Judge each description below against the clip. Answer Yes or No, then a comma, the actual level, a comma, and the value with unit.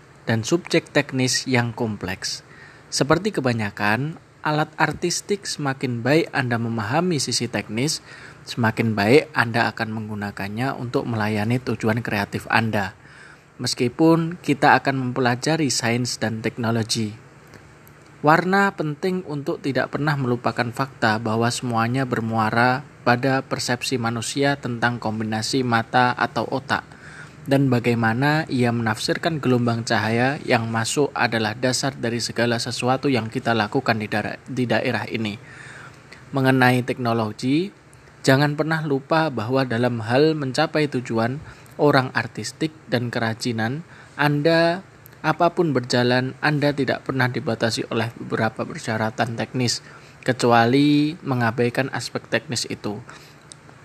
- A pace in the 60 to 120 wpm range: Yes, average, 115 wpm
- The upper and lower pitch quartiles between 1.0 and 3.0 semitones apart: No, average, 4.0 semitones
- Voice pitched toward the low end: Yes, low, 125 Hz